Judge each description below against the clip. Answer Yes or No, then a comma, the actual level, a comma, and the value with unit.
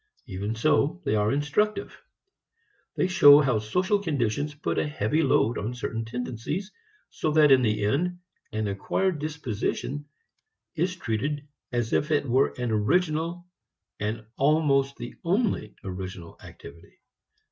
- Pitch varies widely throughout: Yes, wide, 6.1 semitones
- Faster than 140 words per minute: No, slow, 135 wpm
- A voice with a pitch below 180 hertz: Yes, medium, 140 Hz